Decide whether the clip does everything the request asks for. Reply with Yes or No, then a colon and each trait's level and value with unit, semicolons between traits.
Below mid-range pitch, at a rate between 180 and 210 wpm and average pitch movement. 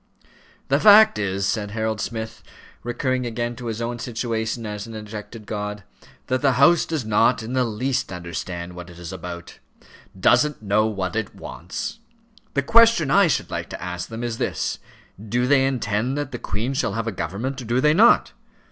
Yes: low, 115 Hz; average, 185 wpm; average, 4.0 semitones